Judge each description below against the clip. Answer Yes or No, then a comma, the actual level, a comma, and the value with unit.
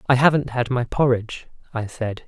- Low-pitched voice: Yes, low, 125 Hz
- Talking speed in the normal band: Yes, average, 185 wpm